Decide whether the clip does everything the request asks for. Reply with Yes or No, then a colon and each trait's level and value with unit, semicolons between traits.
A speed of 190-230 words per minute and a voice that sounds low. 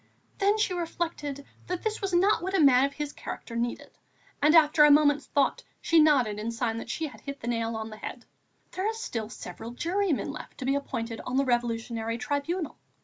No: fast, 205 wpm; very high, 280 Hz